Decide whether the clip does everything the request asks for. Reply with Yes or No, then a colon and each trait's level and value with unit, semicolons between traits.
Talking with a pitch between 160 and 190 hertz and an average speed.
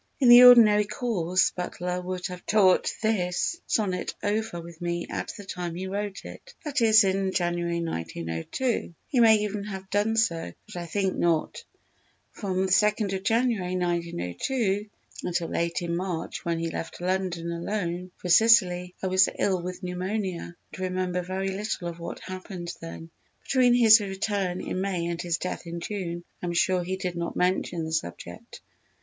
Yes: medium, 185 Hz; average, 165 wpm